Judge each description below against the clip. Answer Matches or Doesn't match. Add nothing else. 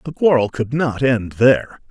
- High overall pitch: Doesn't match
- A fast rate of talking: Doesn't match